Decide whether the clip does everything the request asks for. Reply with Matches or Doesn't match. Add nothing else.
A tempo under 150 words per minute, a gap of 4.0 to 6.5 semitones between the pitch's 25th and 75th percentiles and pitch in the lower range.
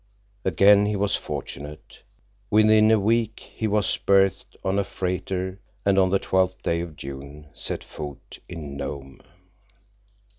Matches